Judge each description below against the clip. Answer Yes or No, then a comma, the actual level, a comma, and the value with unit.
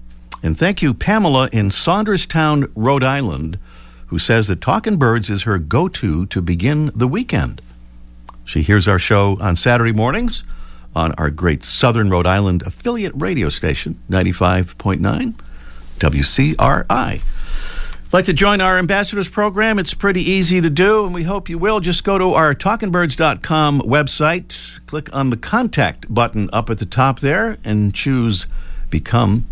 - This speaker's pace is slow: No, average, 150 wpm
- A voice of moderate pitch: No, low, 120 Hz